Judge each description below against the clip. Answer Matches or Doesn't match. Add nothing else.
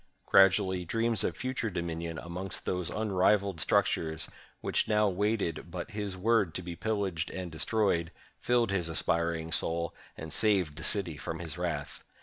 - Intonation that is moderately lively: Matches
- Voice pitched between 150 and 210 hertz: Doesn't match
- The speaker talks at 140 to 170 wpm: Matches